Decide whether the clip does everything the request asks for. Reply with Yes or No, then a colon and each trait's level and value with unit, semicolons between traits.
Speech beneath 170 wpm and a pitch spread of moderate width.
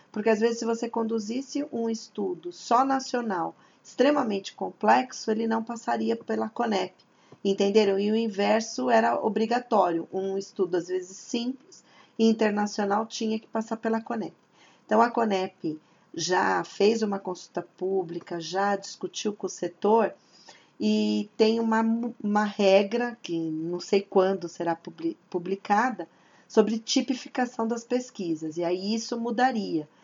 Yes: average, 135 wpm; average, 3.3 semitones